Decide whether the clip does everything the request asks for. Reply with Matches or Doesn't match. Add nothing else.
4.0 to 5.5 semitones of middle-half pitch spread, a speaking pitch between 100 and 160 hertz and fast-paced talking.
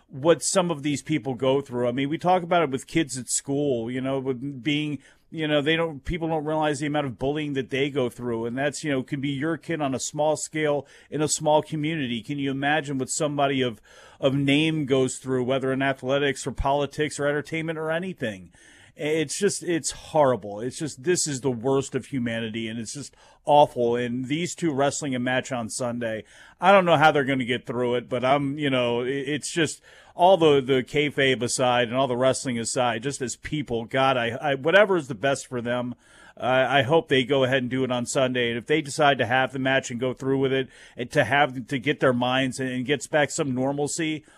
Doesn't match